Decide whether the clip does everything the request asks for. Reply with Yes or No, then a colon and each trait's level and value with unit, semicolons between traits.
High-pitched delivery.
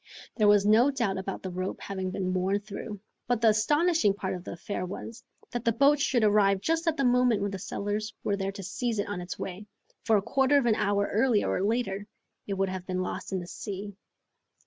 Yes: high, 205 Hz